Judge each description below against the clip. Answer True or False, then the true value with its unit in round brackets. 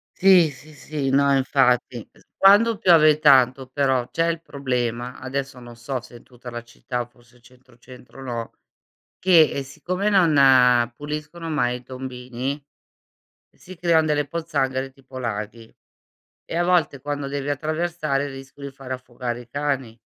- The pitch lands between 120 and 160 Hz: True (135 Hz)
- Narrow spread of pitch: False (3.5 semitones)